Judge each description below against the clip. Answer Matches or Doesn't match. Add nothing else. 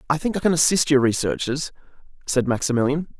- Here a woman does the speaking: Doesn't match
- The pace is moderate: Matches